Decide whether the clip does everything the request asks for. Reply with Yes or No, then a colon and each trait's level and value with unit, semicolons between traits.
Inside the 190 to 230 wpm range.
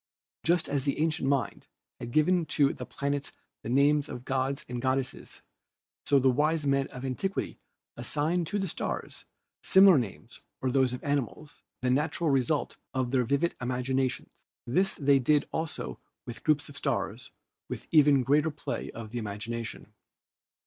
No: average, 160 wpm